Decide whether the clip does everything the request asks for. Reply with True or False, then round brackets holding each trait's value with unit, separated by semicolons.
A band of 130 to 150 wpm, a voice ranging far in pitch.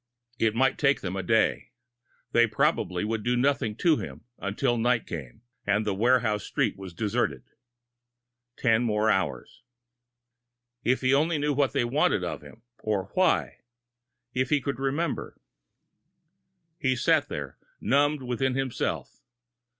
False (140 wpm; 4.3 semitones)